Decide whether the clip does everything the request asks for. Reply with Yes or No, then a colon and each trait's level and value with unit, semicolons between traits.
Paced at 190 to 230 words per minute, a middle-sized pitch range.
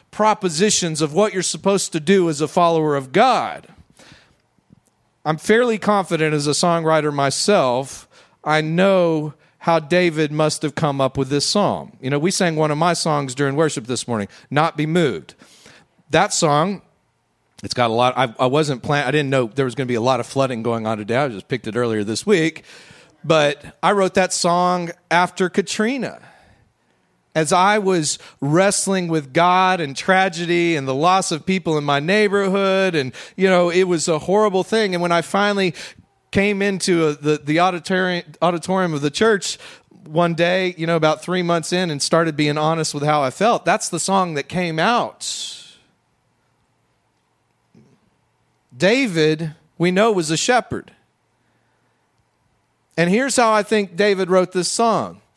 No: average, 170 wpm; average, 4.0 semitones